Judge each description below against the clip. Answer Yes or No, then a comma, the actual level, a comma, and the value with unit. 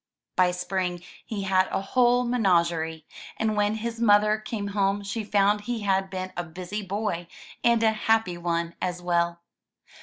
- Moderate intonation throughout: Yes, average, 3.3 semitones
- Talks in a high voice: Yes, high, 195 Hz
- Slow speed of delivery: No, average, 160 wpm